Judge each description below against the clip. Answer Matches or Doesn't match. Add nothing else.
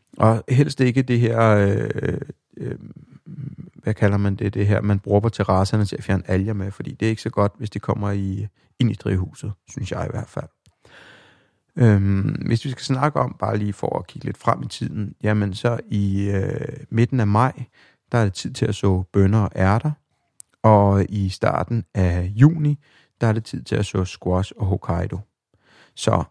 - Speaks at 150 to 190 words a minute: Doesn't match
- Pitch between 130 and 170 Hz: Doesn't match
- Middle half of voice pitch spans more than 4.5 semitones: Doesn't match